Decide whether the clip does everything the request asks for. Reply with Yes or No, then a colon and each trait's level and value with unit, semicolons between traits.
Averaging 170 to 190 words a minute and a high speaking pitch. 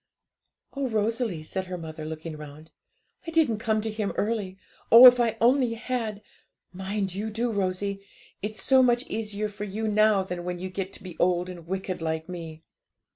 Yes: average, 180 wpm; high, 200 Hz